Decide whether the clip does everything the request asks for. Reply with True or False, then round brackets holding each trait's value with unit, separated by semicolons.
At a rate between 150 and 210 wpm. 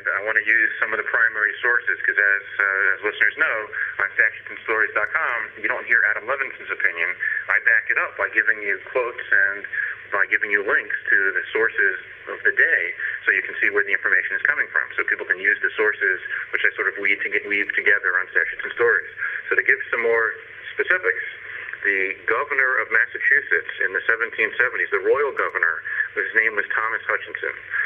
True (190 wpm)